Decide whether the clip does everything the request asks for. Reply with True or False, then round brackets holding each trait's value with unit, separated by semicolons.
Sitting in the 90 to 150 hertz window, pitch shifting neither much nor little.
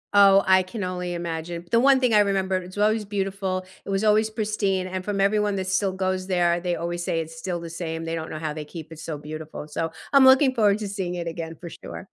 False (185 Hz; 3.2 semitones)